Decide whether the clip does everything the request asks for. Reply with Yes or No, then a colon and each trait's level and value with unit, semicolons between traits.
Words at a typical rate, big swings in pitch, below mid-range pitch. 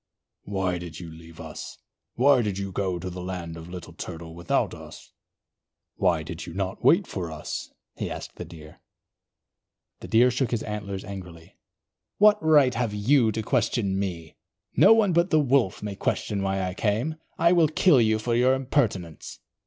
Yes: average, 175 wpm; wide, 6.2 semitones; low, 100 Hz